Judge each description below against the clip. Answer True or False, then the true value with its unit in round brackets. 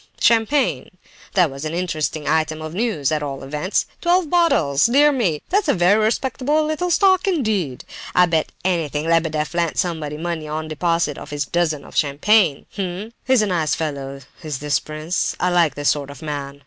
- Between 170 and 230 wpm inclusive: True (175 wpm)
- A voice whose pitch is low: False (165 Hz)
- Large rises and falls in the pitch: True (6.2 semitones)